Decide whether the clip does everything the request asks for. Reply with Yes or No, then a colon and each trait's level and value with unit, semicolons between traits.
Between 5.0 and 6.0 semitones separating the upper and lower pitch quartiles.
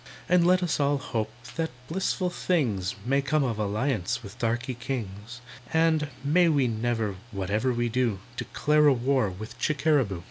Yes: wide, 5.6 semitones